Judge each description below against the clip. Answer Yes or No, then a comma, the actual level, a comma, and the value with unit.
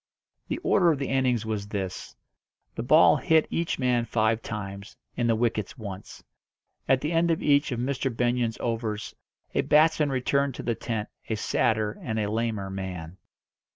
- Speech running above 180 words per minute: No, average, 170 wpm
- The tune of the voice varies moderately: Yes, average, 4.1 semitones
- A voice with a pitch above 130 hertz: No, low, 115 Hz